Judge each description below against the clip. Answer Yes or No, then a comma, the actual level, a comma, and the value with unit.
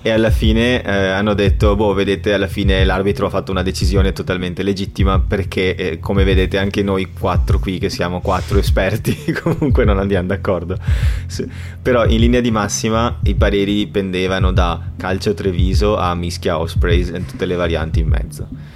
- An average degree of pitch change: No, narrow, 2.0 semitones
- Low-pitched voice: Yes, very low, 95 Hz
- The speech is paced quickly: Yes, fast, 175 wpm